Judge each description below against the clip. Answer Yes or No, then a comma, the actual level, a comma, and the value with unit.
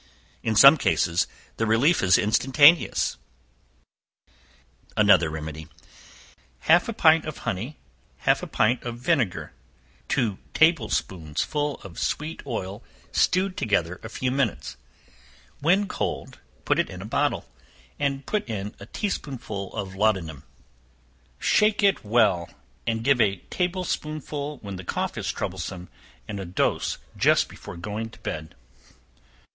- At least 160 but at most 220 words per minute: No, slow, 135 wpm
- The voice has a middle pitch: No, low, 115 Hz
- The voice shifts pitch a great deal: Yes, wide, 7.8 semitones